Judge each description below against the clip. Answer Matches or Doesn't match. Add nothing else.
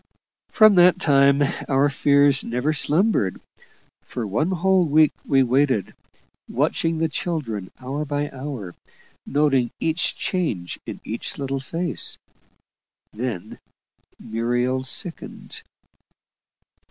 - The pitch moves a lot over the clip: Doesn't match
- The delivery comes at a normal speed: Doesn't match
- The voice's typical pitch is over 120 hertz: Matches